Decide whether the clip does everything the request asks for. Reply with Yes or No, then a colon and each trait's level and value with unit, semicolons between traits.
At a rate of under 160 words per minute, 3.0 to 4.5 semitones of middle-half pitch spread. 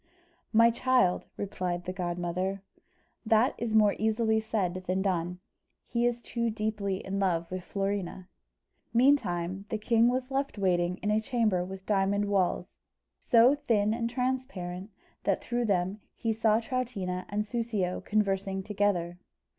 Yes: average, 140 wpm; average, 3.8 semitones